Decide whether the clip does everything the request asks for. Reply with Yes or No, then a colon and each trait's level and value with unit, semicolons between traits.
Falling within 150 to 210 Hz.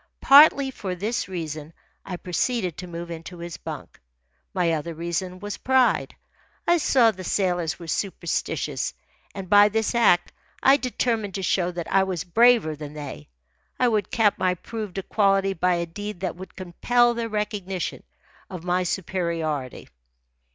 Yes: medium, 185 Hz